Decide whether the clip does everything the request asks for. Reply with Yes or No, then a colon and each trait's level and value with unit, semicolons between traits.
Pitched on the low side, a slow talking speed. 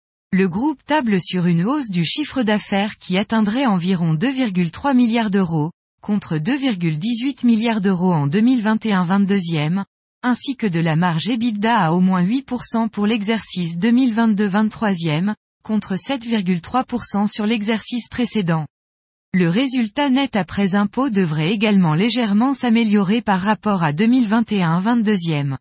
No: high, 210 Hz; slow, 120 wpm